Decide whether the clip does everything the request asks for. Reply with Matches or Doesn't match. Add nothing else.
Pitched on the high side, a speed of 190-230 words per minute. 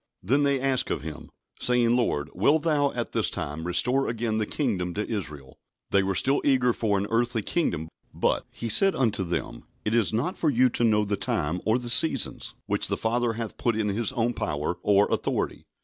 Doesn't match